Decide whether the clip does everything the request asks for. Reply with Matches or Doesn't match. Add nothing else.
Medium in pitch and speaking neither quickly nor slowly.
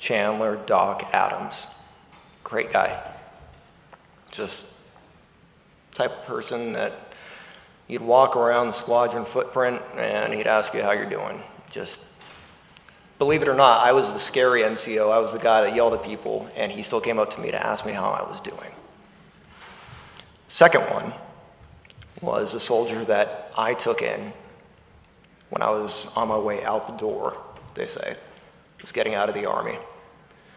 Doesn't match